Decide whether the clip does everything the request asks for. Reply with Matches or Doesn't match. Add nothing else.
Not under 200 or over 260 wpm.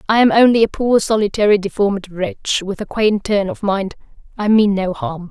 Matches